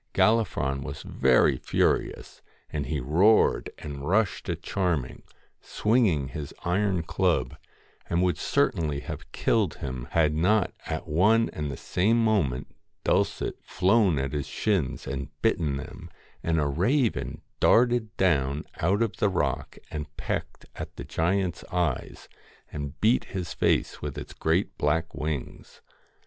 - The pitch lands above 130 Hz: No, very low, 80 Hz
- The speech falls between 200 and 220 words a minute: No, average, 140 wpm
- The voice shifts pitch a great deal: Yes, wide, 5.7 semitones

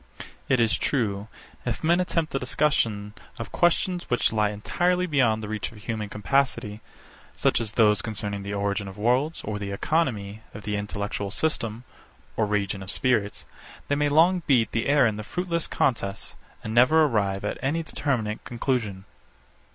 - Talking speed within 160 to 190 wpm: Yes, average, 165 wpm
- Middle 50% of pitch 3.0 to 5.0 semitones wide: No, wide, 5.5 semitones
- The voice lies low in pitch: Yes, low, 110 Hz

